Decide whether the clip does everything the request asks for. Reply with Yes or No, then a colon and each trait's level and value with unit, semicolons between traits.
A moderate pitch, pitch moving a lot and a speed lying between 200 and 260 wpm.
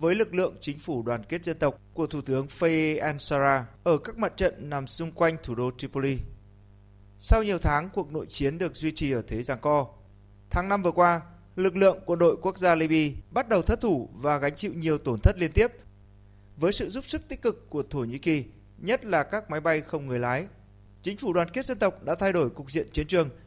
Yes: medium, 150 Hz; wide, 6.0 semitones; average, 235 wpm